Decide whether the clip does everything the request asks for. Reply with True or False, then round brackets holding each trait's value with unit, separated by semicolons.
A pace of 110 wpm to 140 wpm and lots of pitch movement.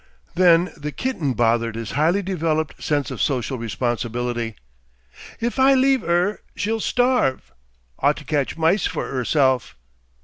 True (135 wpm; 7.6 semitones)